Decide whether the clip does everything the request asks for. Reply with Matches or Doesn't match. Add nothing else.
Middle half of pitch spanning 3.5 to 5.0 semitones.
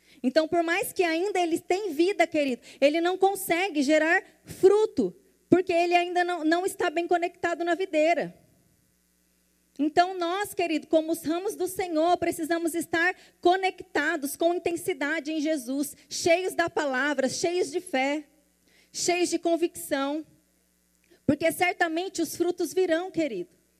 Doesn't match